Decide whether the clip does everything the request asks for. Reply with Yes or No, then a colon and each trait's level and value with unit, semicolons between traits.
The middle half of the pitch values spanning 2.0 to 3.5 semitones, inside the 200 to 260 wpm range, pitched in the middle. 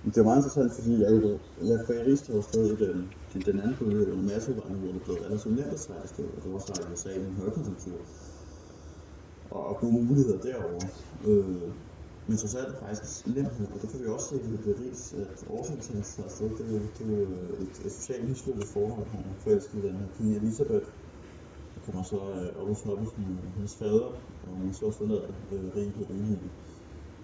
No: average, 3.1 semitones; fast, 225 wpm; low, 100 Hz